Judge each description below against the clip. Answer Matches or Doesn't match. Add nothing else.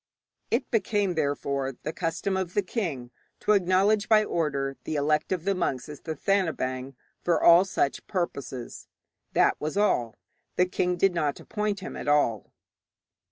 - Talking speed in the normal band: Matches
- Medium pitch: Matches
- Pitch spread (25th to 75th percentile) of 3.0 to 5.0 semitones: Doesn't match